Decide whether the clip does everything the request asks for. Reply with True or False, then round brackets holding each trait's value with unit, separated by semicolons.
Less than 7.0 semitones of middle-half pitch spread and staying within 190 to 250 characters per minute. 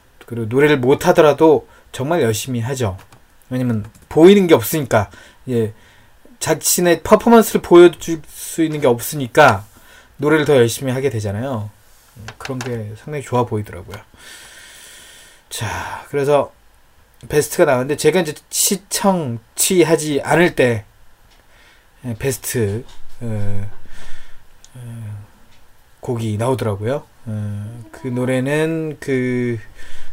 True (5.2 semitones; 235 characters per minute)